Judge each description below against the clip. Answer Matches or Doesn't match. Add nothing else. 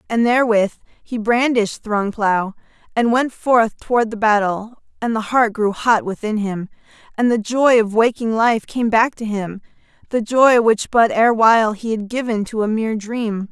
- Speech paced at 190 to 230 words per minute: Doesn't match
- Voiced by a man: Doesn't match